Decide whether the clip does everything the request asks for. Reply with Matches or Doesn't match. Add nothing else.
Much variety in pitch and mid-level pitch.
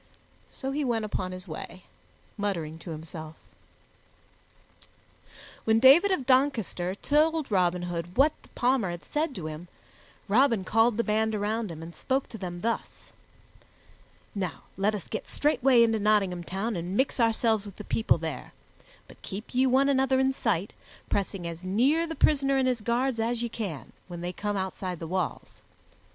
Doesn't match